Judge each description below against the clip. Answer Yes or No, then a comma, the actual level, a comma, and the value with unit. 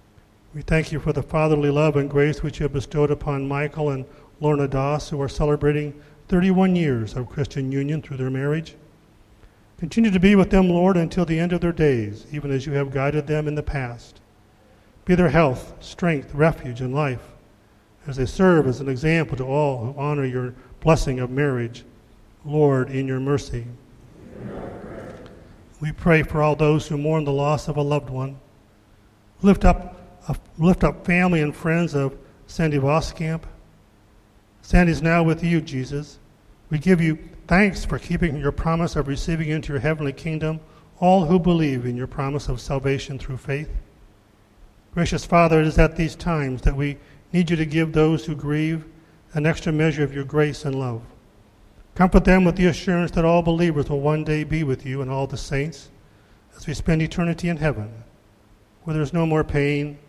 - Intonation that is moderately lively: Yes, average, 3.6 semitones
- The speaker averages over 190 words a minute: No, average, 185 wpm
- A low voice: No, medium, 145 Hz